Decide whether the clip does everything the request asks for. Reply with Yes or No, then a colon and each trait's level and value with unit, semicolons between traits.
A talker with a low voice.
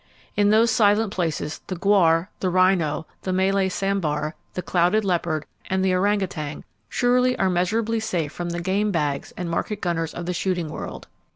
No: medium, 185 Hz